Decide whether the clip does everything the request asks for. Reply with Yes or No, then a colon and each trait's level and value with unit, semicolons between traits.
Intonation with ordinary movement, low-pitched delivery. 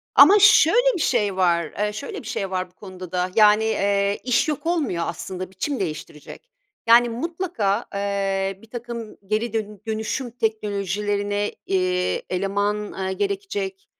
No: average, 3.9 semitones; high, 210 Hz